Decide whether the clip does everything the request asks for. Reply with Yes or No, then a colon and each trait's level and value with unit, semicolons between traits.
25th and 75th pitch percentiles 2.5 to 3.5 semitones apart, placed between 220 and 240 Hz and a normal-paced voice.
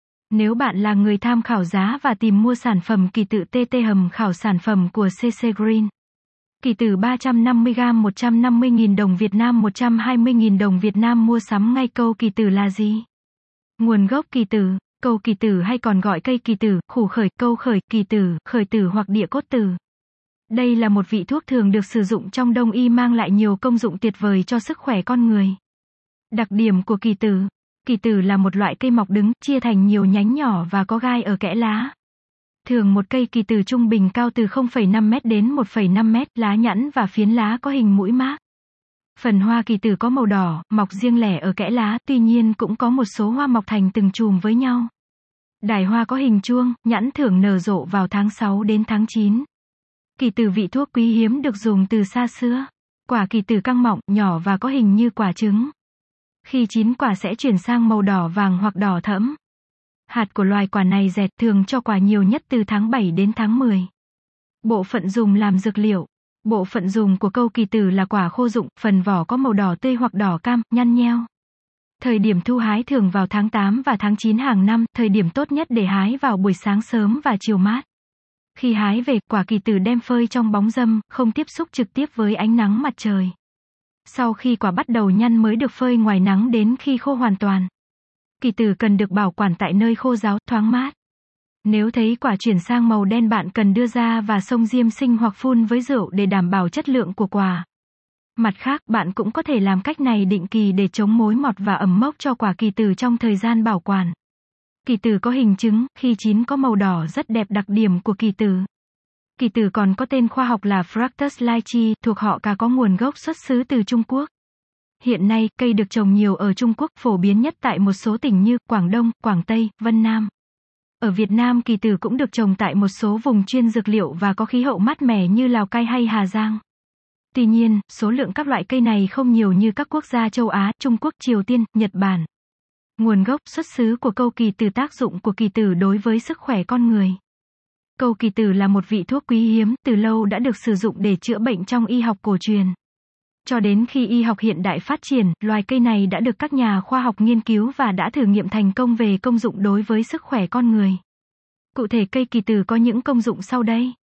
Yes: average, 2.9 semitones; high, 225 Hz; average, 225 wpm